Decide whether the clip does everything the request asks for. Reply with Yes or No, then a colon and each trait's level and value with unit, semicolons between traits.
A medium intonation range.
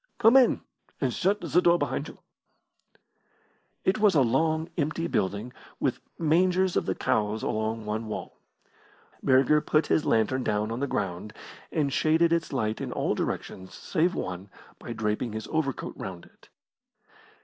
No: wide, 7.5 semitones